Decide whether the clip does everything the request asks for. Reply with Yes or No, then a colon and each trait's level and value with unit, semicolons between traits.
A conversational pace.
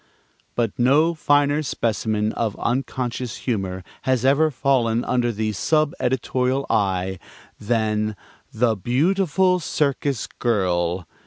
No: slow, 105 wpm